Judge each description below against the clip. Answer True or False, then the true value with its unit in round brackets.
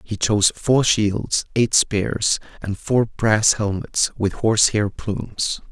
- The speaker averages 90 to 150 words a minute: True (145 wpm)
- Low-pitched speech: True (105 Hz)